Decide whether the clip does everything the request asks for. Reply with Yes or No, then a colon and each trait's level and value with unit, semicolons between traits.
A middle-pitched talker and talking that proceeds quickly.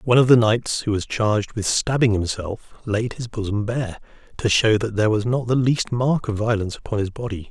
No: low, 110 Hz; fast, 225 wpm